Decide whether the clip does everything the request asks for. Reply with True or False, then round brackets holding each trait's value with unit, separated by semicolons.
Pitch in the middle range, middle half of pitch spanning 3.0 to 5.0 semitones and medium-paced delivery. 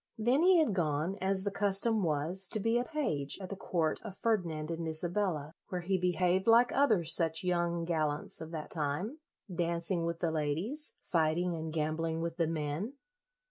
True (170 Hz; 3.6 semitones; 180 wpm)